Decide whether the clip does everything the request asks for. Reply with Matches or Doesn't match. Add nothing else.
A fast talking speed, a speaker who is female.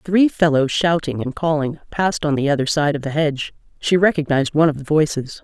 Matches